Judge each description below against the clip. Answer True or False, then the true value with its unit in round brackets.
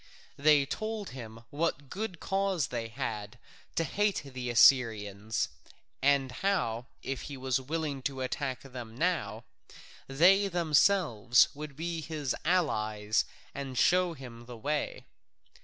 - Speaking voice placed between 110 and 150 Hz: True (140 Hz)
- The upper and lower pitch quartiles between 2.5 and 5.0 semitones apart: False (5.6 semitones)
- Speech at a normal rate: False (125 wpm)